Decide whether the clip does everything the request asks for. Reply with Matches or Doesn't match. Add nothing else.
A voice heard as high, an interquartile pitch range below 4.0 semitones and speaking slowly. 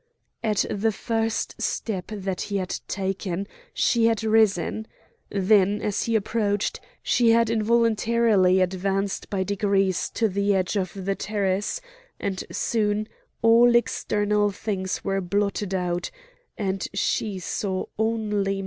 Matches